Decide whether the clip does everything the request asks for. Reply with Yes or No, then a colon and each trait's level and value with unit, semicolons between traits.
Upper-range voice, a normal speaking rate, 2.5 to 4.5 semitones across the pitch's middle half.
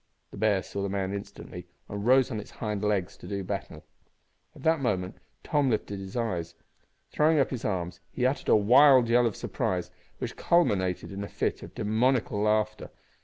No: low, 105 Hz; average, 185 wpm; average, 4.1 semitones